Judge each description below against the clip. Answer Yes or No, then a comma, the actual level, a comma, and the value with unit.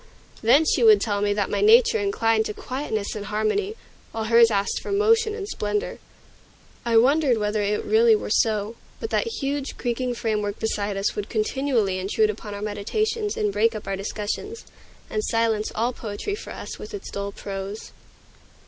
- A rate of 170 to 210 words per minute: Yes, average, 175 wpm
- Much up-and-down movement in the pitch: Yes, wide, 6.8 semitones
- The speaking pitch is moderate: No, high, 225 Hz